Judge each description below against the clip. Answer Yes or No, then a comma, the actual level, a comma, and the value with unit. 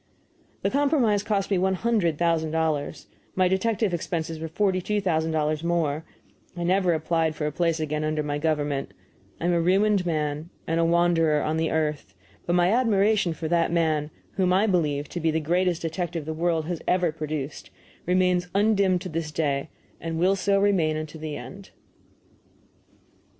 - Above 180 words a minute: No, average, 175 wpm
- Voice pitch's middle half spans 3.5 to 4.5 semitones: No, average, 3.0 semitones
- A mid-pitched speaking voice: Yes, medium, 165 Hz